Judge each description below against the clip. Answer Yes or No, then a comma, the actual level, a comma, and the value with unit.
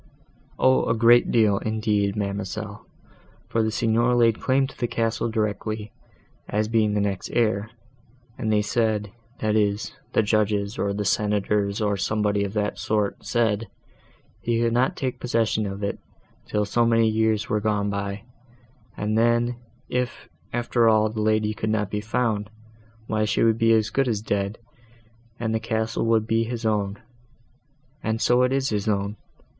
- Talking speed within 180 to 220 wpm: No, average, 165 wpm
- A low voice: Yes, low, 110 Hz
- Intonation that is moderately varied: No, narrow, 1.7 semitones